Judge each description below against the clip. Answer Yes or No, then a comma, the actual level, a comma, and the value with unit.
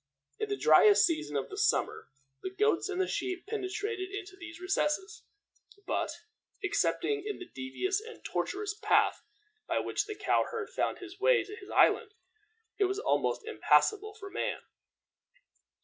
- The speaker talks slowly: No, average, 155 wpm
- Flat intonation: Yes, narrow, 2.2 semitones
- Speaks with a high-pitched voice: Yes, very high, 400 Hz